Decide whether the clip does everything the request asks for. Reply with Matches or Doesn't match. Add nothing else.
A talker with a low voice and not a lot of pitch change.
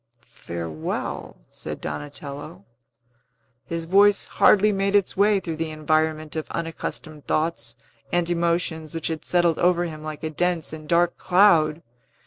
Doesn't match